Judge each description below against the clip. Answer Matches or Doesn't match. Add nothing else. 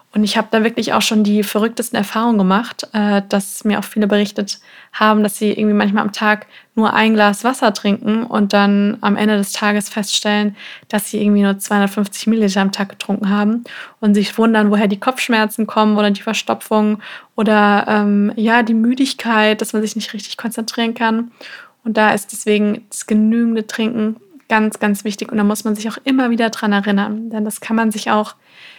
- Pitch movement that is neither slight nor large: Doesn't match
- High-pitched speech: Matches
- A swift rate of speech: Matches